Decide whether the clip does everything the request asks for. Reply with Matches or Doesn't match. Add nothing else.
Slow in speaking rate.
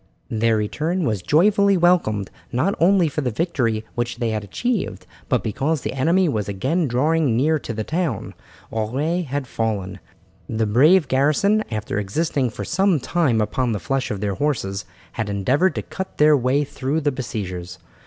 Doesn't match